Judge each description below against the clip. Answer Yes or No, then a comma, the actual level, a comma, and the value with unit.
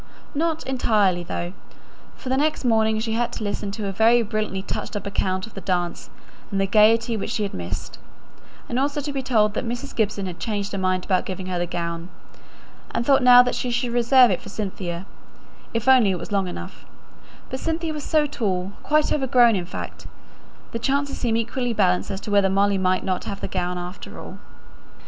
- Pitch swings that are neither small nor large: Yes, average, 4.6 semitones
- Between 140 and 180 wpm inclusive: No, fast, 205 wpm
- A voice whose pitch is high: Yes, high, 215 Hz